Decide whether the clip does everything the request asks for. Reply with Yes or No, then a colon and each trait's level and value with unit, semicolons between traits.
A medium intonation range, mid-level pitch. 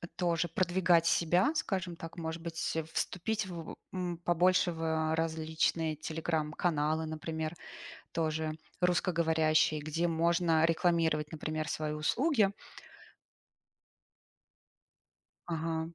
No: narrow, 1.6 semitones; medium, 165 Hz